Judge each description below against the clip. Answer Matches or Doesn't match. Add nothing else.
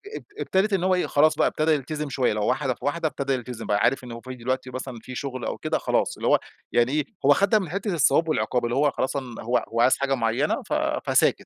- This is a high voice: Doesn't match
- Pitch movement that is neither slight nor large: Matches